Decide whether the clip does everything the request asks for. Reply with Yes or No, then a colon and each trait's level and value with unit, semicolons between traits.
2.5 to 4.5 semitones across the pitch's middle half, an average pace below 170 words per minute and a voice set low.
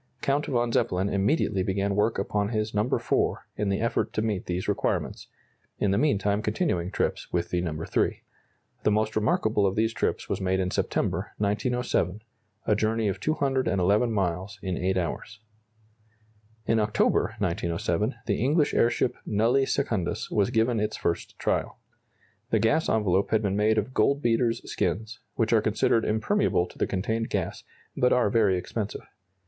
Yes: average, 2.8 semitones; average, 160 wpm; low, 105 Hz